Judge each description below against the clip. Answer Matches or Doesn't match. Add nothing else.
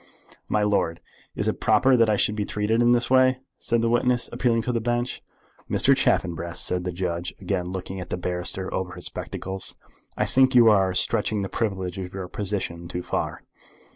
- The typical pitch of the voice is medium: Doesn't match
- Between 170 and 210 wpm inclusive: Matches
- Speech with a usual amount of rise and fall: Matches